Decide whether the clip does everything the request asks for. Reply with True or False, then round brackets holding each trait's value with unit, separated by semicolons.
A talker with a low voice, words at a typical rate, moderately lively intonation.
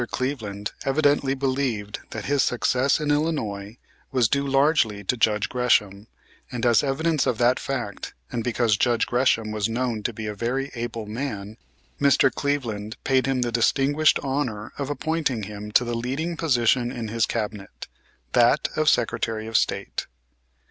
True (120 Hz; 155 wpm; 4.0 semitones)